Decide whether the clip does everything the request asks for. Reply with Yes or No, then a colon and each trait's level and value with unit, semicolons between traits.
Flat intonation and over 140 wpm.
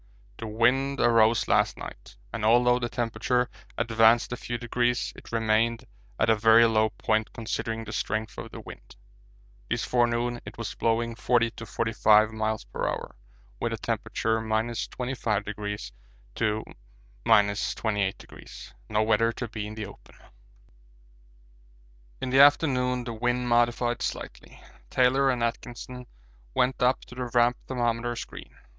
No: narrow, 1.8 semitones; slow, 135 wpm